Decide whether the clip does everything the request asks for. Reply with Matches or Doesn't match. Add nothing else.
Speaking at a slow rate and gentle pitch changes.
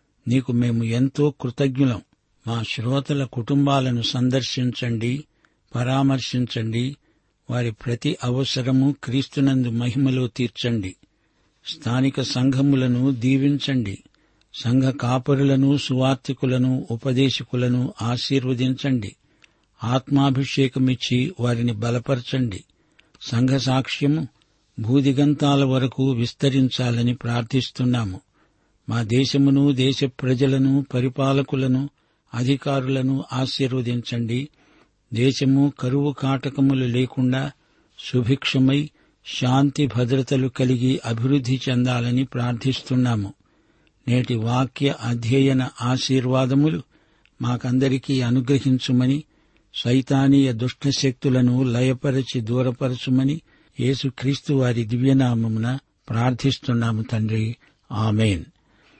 Matches